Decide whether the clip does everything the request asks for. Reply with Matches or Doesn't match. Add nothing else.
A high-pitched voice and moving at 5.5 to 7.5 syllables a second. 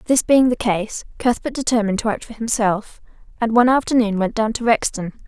Matches